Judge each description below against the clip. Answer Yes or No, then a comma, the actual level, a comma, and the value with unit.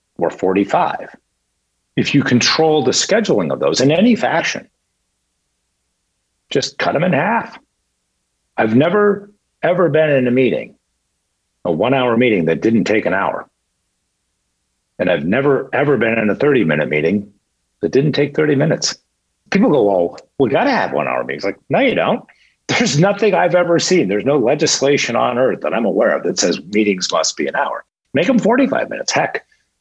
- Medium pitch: No, low, 125 Hz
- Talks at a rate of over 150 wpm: Yes, average, 180 wpm